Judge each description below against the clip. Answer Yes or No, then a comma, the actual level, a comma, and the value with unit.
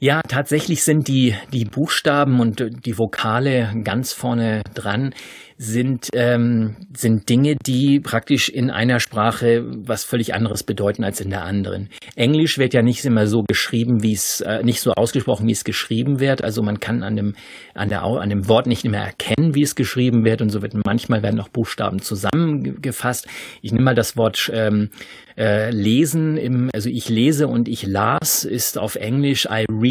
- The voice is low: Yes, low, 115 Hz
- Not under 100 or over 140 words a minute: No, average, 185 wpm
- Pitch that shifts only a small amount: No, average, 3.2 semitones